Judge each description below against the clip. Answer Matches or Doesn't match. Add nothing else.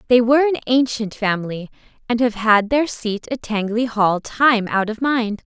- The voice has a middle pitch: Doesn't match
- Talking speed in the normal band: Matches